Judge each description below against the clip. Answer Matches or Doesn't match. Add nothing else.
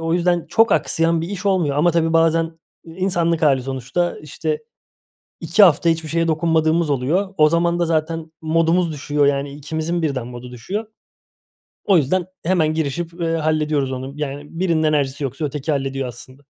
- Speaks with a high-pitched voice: Doesn't match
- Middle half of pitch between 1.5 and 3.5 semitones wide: Matches